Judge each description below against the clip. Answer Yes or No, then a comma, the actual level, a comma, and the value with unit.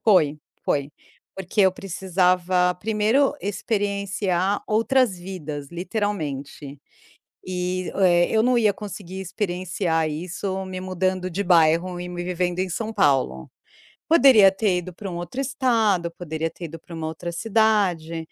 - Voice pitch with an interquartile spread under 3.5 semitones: Yes, average, 3.1 semitones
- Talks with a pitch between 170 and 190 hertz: Yes, medium, 185 Hz